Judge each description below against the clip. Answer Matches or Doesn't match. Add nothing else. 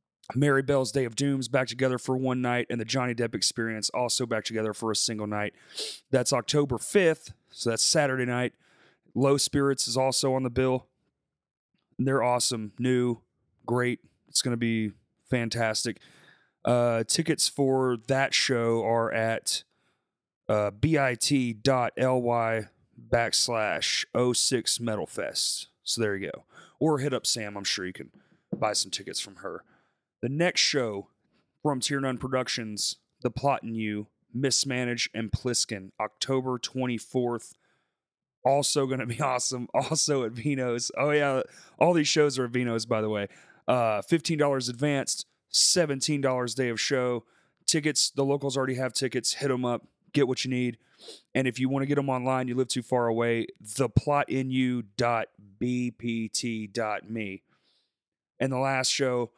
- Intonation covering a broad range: Doesn't match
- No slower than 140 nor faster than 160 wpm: Matches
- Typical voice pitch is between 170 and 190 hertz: Doesn't match